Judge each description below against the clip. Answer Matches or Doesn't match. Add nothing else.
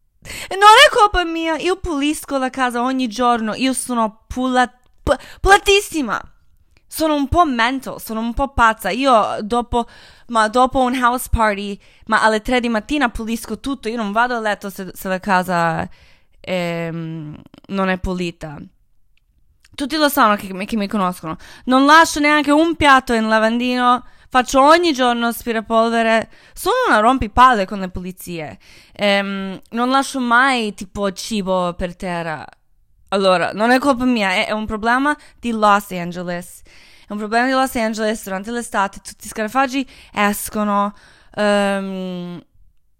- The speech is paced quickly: Doesn't match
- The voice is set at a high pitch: Matches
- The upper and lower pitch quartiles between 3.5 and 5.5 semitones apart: Matches